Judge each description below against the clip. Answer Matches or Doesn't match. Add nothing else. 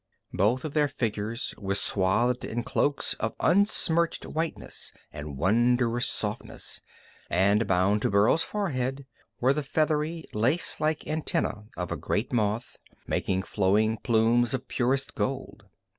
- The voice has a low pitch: Matches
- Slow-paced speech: Matches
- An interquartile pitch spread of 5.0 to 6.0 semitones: Matches